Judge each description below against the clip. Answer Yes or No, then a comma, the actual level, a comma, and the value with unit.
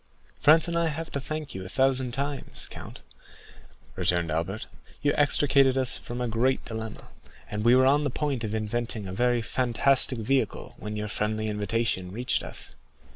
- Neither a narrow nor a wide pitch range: Yes, average, 4.3 semitones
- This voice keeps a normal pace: Yes, average, 175 wpm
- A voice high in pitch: No, low, 120 Hz